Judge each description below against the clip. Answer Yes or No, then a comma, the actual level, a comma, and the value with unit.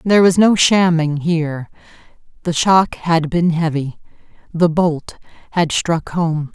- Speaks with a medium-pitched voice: Yes, medium, 165 Hz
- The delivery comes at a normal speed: No, slow, 120 wpm